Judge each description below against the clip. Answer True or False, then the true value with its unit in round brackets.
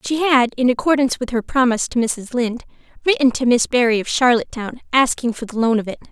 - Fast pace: True (215 wpm)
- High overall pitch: True (245 Hz)